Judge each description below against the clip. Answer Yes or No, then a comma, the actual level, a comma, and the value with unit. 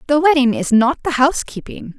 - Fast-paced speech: No, average, 180 wpm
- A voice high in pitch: Yes, very high, 270 Hz